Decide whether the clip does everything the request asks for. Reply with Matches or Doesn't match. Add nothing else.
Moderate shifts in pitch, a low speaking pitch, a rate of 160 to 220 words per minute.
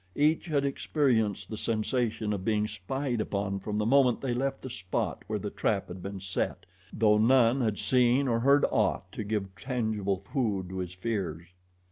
Matches